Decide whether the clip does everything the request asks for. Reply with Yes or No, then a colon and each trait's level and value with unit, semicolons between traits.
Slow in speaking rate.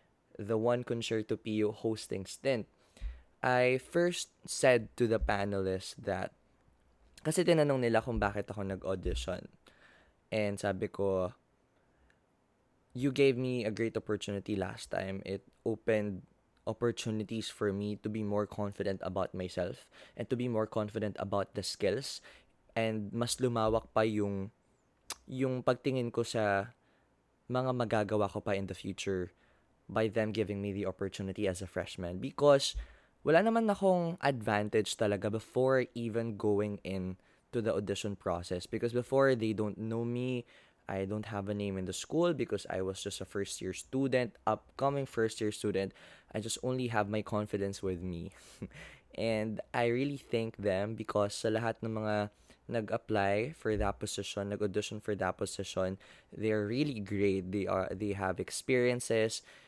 No: average, 150 wpm